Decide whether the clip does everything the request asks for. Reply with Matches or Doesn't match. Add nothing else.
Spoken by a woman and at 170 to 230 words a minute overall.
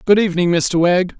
Doesn't match